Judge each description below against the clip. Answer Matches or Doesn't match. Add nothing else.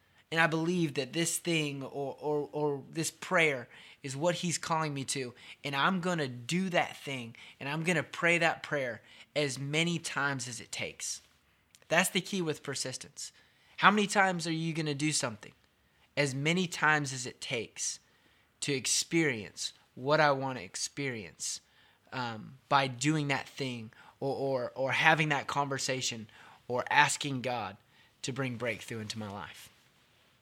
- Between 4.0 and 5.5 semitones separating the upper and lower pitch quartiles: Matches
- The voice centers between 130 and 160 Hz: Matches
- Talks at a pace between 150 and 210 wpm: Matches